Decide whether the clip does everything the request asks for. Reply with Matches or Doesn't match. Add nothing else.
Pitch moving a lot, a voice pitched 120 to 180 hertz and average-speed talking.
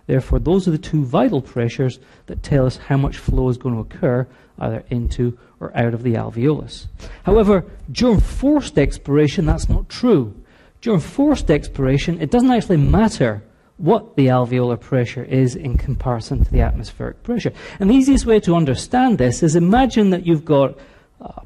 Matches